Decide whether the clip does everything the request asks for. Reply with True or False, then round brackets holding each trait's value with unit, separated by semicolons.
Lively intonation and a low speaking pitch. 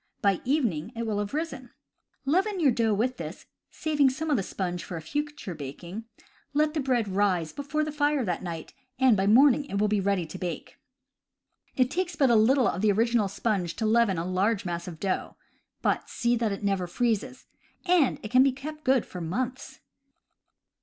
False (6.0 semitones; 230 Hz)